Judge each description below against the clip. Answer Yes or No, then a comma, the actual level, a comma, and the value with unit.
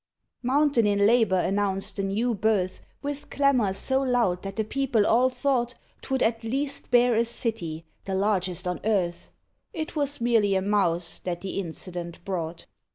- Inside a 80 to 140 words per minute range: No, average, 160 wpm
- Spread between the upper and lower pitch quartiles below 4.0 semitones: No, average, 4.6 semitones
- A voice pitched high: Yes, high, 215 Hz